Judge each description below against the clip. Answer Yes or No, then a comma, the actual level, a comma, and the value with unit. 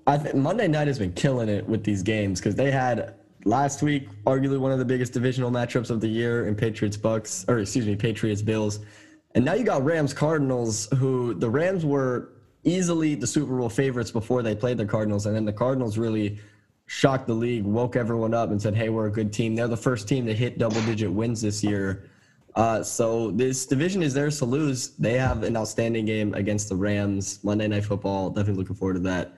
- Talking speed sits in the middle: No, fast, 220 wpm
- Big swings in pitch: No, average, 3.8 semitones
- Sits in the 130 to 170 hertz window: No, low, 115 Hz